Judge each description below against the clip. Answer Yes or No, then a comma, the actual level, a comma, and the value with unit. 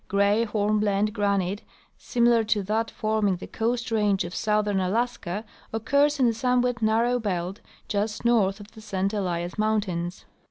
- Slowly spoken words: No, average, 150 wpm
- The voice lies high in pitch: Yes, high, 215 Hz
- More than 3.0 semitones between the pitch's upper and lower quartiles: No, narrow, 2.4 semitones